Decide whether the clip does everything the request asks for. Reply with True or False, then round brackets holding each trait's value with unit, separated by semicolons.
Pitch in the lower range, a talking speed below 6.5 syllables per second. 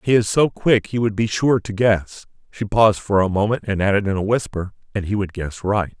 True (105 Hz; 5.3 syllables/s)